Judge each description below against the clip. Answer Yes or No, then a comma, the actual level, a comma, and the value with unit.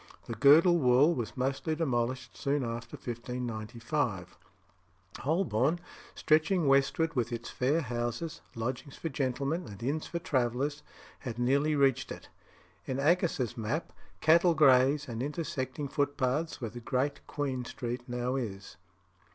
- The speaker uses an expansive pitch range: No, average, 3.8 semitones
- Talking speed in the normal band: No, slow, 125 wpm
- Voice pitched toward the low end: Yes, low, 130 Hz